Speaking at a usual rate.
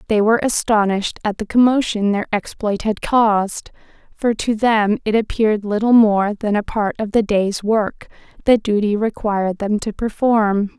Yes: average, 165 wpm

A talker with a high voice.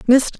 Yes: very high, 260 Hz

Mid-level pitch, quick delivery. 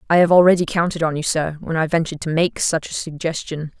Yes: medium, 160 Hz; fast, 235 wpm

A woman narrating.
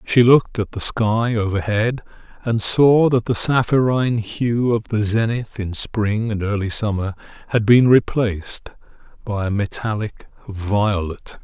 No: male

